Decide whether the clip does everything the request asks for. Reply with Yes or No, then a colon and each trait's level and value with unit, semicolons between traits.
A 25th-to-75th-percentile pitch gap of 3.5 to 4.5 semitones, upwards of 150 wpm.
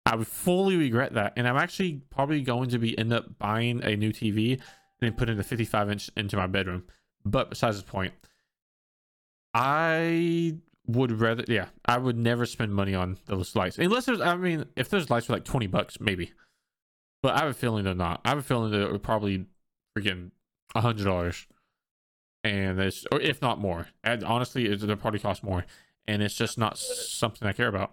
Yes: average, 4.0 semitones; fast, 205 wpm